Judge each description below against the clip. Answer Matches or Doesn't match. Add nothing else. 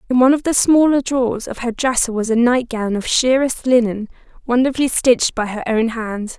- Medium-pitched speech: Doesn't match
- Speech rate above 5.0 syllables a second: Matches